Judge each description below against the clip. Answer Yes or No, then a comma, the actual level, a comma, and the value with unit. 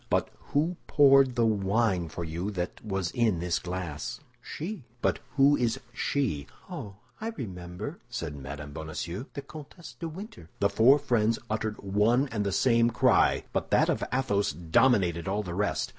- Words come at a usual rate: Yes, average, 165 wpm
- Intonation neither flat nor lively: No, wide, 6.9 semitones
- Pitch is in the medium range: No, low, 105 Hz